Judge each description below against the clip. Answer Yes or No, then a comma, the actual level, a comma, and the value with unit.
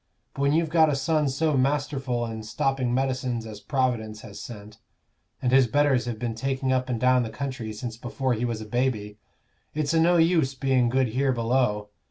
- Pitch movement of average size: Yes, average, 3.1 semitones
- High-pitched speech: No, low, 130 Hz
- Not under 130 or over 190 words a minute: No, average, 200 wpm